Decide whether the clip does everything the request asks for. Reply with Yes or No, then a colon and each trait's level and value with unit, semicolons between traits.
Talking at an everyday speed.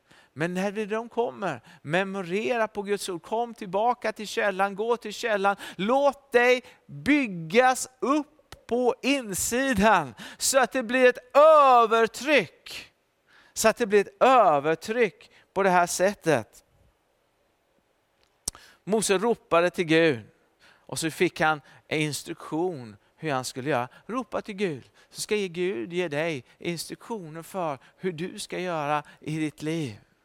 Yes: average, 135 wpm